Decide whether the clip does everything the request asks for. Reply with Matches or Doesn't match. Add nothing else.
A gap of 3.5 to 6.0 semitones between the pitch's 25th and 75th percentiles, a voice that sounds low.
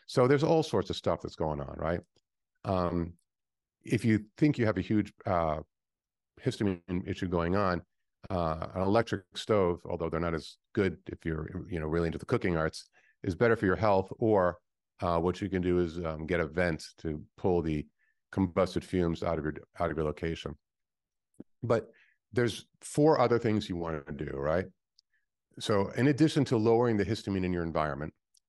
Matches